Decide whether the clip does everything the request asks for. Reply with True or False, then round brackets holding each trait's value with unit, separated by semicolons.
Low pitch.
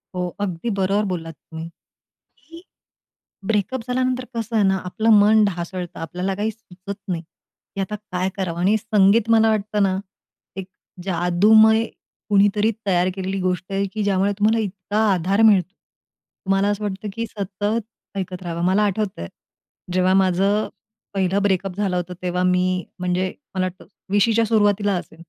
False (195 Hz)